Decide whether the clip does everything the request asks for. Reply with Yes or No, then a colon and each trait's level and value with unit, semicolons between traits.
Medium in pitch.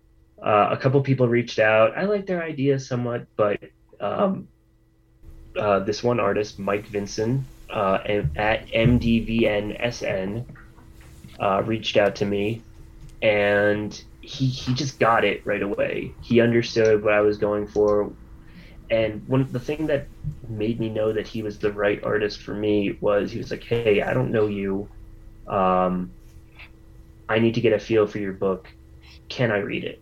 No: low, 110 Hz